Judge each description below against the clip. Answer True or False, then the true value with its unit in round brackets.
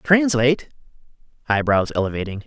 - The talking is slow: True (75 wpm)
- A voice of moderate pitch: False (130 Hz)